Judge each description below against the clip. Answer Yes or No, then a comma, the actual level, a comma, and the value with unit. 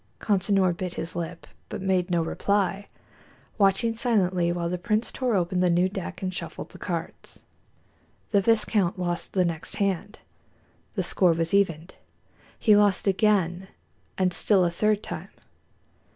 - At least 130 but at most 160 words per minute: Yes, average, 150 wpm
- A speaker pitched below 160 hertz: No, medium, 185 Hz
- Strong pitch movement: No, average, 2.7 semitones